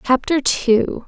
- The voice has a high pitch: Yes, very high, 265 Hz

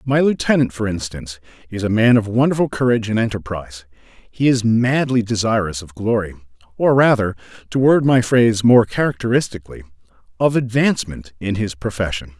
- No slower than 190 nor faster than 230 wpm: No, average, 150 wpm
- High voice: No, low, 110 Hz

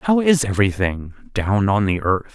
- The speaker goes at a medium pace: Yes, average, 180 wpm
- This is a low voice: Yes, low, 110 Hz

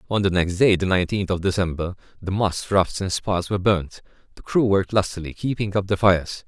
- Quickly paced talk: Yes, fast, 215 wpm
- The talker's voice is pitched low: Yes, very low, 95 Hz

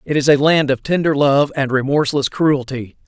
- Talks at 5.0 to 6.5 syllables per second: Yes, 5.2 syllables/s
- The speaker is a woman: No, male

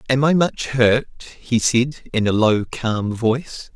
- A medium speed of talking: Yes, average, 175 wpm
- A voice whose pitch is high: No, low, 120 Hz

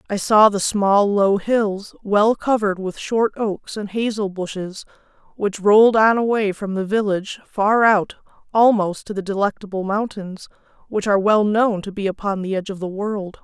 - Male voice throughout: No, female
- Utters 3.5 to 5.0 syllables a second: Yes, 4.8 syllables/s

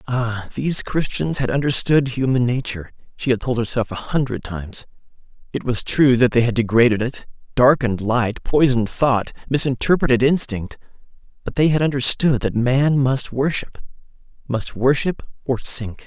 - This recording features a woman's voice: No, male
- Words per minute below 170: Yes, average, 150 wpm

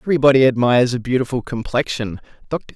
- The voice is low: Yes, low, 125 Hz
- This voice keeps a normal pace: No, slow, 130 wpm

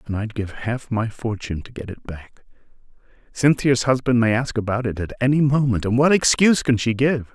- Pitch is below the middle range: Yes, low, 120 Hz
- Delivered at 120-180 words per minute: No, fast, 205 wpm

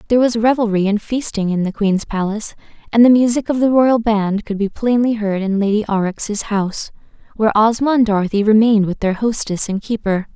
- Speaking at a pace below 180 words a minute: No, average, 195 wpm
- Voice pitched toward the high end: Yes, high, 215 Hz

